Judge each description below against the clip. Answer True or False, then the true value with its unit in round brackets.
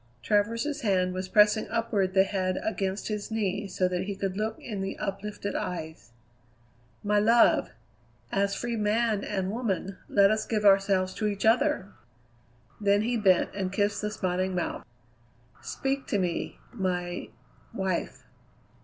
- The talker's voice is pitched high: True (200 Hz)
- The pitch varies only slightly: True (2.3 semitones)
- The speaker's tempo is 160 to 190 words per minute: False (145 wpm)